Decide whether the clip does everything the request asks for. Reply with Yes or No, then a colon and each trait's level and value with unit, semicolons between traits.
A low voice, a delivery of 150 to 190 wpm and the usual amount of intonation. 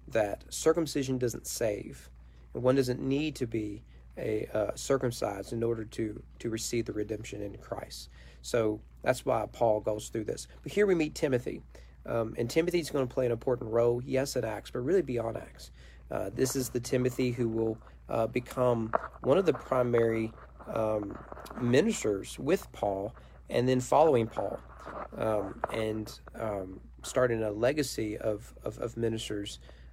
Yes: low, 115 Hz; average, 160 wpm; average, 3.3 semitones